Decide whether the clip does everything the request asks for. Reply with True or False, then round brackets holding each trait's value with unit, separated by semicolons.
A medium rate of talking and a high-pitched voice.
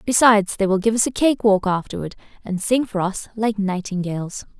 True (195 wpm; 205 Hz)